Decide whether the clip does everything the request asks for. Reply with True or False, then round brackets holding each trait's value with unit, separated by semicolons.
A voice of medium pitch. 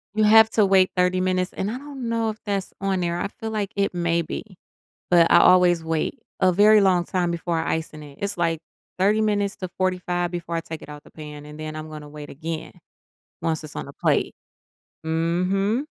True (180 Hz)